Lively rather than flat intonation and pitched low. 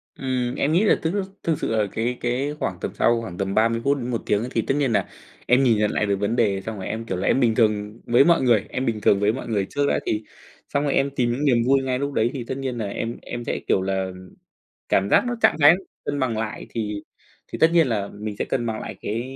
No: average, 3.9 semitones; low, 120 Hz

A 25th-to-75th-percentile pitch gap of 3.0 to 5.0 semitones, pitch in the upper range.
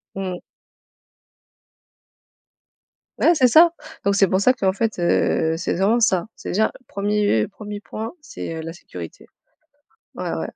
Yes: average, 3.7 semitones; high, 200 Hz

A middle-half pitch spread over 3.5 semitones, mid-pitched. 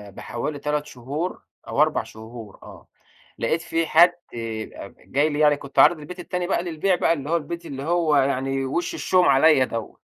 Yes: average, 4.0 semitones; medium, 150 Hz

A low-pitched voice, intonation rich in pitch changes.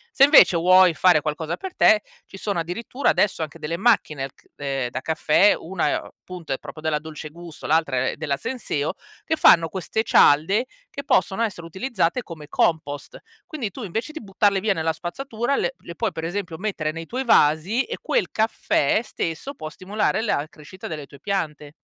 No: medium, 175 Hz; wide, 5.8 semitones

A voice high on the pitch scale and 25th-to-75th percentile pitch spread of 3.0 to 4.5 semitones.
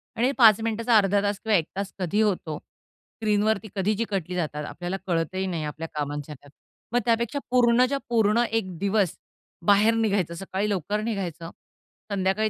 Yes: high, 200 Hz; average, 3.8 semitones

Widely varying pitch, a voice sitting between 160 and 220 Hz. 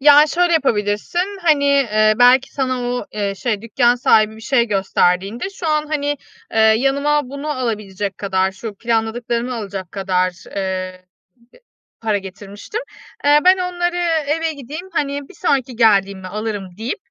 No: wide, 5.9 semitones; high, 235 Hz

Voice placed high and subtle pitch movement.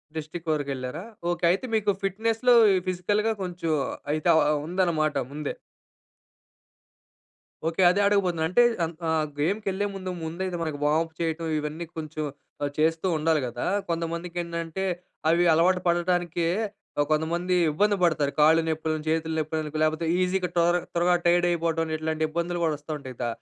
No: medium, 165 Hz; narrow, 2.3 semitones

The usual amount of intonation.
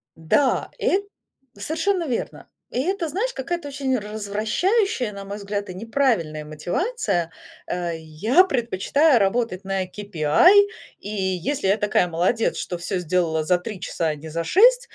No: wide, 8.2 semitones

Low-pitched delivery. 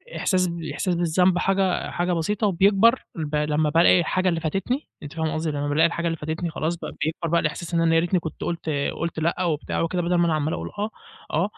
No: medium, 170 Hz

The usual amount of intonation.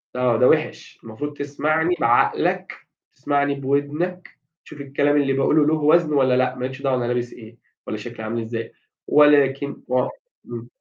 Yes: average, 3.1 semitones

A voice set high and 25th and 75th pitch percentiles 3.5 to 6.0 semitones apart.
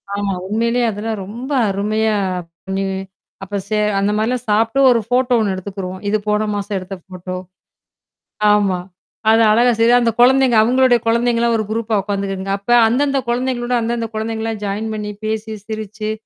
No: high, 220 Hz; average, 2.7 semitones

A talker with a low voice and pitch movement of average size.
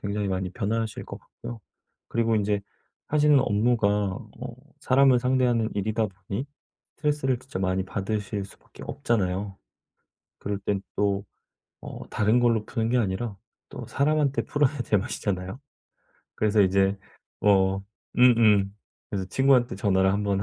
Yes: low, 105 Hz; average, 3.8 semitones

